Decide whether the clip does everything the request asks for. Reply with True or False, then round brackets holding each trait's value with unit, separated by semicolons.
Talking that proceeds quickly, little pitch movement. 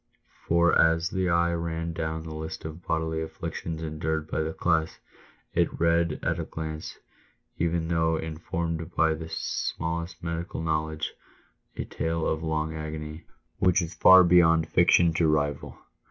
False (155 wpm; 1.1 semitones)